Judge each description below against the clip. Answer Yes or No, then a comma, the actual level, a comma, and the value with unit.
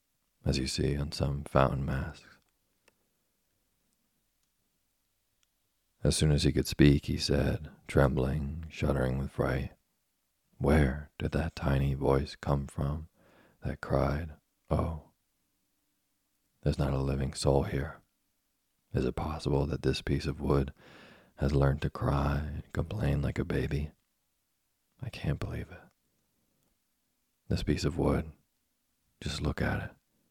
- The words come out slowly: Yes, slow, 125 wpm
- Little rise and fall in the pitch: Yes, narrow, 1.8 semitones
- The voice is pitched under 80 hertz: Yes, very low, 70 Hz